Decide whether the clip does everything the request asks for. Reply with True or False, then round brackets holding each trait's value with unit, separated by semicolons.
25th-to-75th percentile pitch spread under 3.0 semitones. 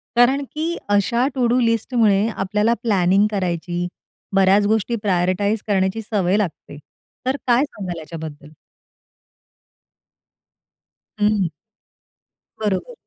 False (3.8 semitones)